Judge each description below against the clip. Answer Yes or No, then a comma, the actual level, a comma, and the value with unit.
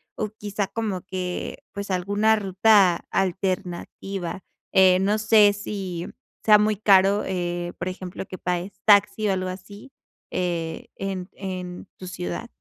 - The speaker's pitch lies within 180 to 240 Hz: Yes, high, 190 Hz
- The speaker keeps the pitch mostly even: Yes, narrow, 2.2 semitones